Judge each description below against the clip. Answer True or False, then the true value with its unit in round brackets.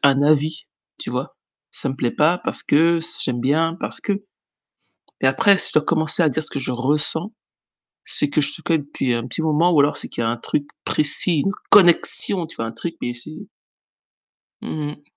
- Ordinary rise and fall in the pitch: True (3.3 semitones)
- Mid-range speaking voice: True (150 Hz)